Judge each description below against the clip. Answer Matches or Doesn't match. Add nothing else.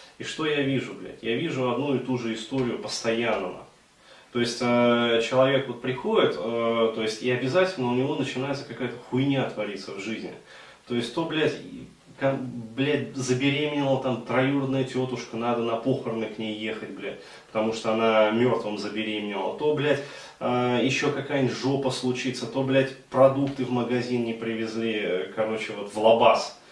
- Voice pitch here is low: Matches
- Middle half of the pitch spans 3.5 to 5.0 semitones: Doesn't match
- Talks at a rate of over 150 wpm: Matches